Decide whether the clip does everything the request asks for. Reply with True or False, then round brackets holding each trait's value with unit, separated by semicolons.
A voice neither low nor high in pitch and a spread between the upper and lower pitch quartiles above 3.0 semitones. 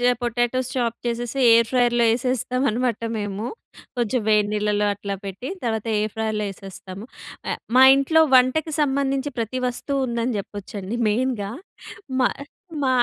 False (235 Hz; 3.4 semitones)